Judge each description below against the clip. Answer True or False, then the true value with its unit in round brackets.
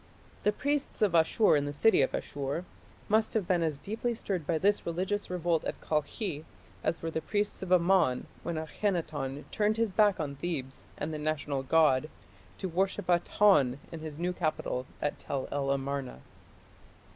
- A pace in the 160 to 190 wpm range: True (170 wpm)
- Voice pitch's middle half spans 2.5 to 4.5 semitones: False (5.1 semitones)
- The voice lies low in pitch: False (165 Hz)